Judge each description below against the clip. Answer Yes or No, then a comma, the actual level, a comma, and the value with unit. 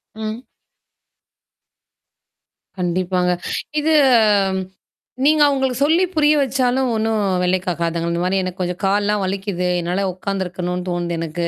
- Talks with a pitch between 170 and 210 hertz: Yes, high, 190 Hz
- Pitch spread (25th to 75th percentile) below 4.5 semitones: No, average, 5.2 semitones